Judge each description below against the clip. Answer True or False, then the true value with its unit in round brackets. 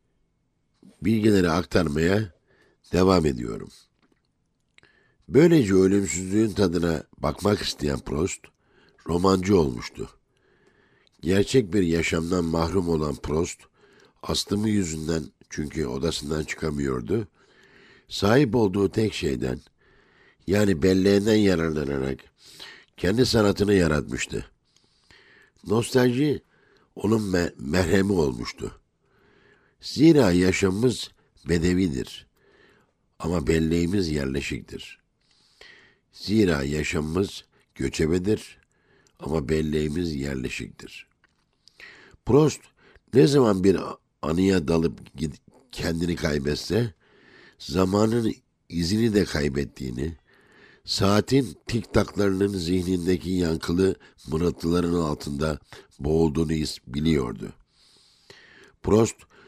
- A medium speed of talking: False (70 wpm)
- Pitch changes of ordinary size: True (4.3 semitones)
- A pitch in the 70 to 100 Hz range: True (90 Hz)